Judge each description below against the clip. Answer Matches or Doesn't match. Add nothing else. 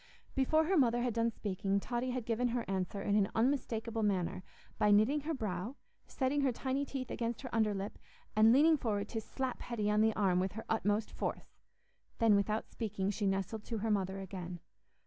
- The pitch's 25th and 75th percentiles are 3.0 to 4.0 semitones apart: Matches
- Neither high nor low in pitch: Doesn't match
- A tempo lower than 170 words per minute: Doesn't match